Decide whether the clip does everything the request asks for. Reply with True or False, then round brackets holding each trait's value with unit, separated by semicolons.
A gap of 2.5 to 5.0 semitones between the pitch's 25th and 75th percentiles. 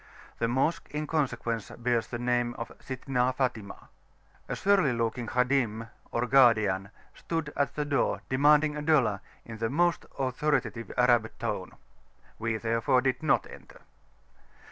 True (3.7 semitones)